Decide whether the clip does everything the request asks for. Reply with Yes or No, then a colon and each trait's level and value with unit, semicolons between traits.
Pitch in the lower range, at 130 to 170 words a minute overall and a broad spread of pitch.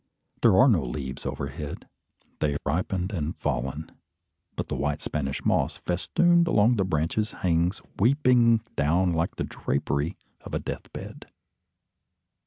Yes: very low, 85 Hz; slow, 135 wpm; wide, 6.7 semitones